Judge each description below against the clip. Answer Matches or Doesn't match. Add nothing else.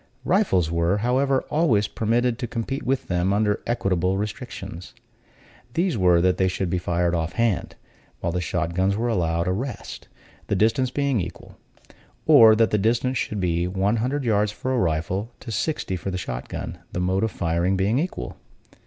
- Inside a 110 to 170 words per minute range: Doesn't match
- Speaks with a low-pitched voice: Matches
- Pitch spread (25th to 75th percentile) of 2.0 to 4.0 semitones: Doesn't match